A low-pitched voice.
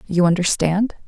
No: medium, 185 Hz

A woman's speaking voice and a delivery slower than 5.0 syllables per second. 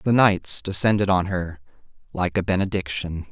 No: male; 4.7 syllables/s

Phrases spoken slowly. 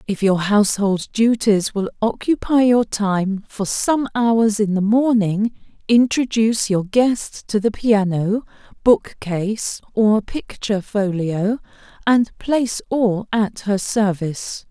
Yes: slow, 125 wpm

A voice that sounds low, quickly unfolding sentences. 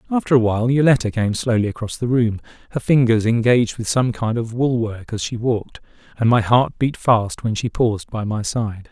Yes: low, 115 Hz; fast, 215 wpm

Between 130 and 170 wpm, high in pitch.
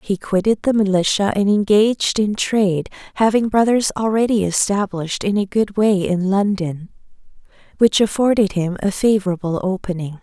Yes: average, 140 wpm; high, 200 Hz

